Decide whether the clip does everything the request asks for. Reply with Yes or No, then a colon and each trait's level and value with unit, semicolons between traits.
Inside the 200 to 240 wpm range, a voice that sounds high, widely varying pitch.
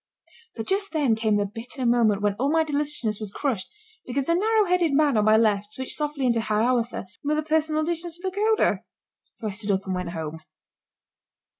Yes: fast, 205 wpm; very high, 250 Hz; wide, 6.6 semitones